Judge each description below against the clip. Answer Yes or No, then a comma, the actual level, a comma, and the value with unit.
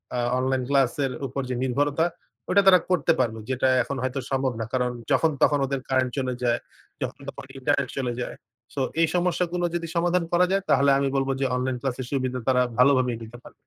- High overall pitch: No, low, 135 Hz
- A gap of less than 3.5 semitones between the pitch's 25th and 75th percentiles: No, average, 3.8 semitones